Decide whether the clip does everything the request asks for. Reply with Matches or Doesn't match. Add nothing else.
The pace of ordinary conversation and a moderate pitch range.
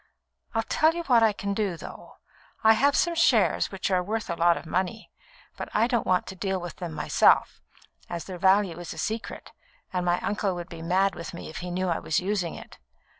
Doesn't match